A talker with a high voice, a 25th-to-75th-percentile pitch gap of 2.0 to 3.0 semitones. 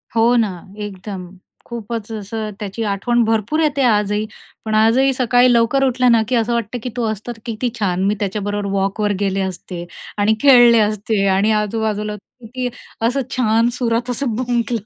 Yes: high, 225 Hz; average, 2.7 semitones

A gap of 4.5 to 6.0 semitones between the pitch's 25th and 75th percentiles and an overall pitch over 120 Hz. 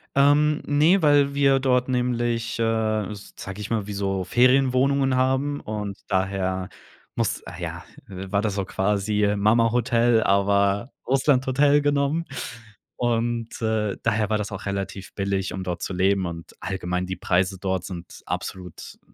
No: average, 4.9 semitones; low, 110 Hz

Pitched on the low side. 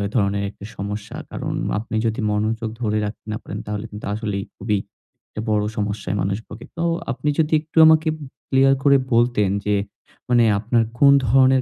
Yes: low, 110 Hz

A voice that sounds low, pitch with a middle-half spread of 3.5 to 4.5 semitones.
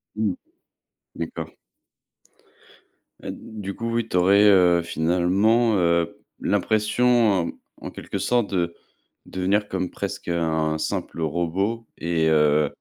Yes: very low, 90 Hz; average, 4.1 semitones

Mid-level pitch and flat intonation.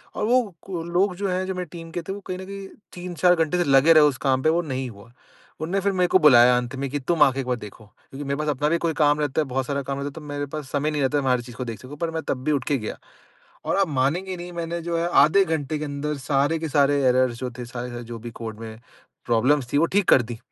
No: medium, 145 Hz; average, 4.6 semitones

